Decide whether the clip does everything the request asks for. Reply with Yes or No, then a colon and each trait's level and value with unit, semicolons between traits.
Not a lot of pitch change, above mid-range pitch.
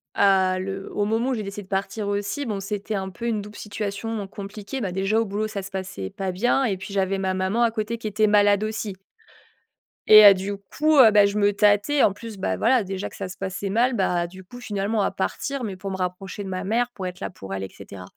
Yes: narrow, 2.1 semitones; high, 200 Hz